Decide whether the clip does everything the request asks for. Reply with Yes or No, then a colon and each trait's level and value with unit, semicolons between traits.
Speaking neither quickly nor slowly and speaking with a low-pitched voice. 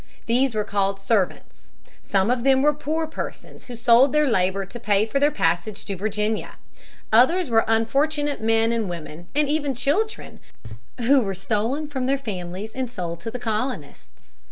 No: average, 170 wpm; high, 225 Hz